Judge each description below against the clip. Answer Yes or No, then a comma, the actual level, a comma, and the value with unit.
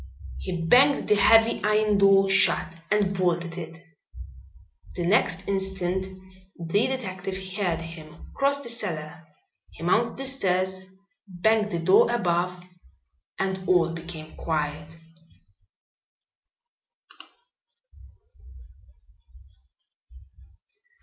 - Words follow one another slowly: Yes, slow, 90 wpm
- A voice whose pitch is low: No, medium, 185 Hz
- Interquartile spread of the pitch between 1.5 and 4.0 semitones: Yes, average, 3.7 semitones